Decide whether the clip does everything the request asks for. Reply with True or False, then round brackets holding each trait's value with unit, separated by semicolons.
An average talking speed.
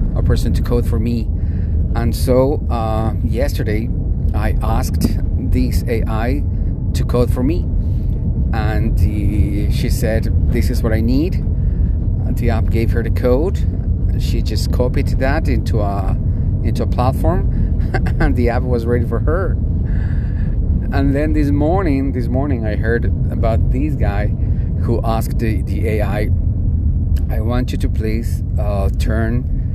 True (145 wpm)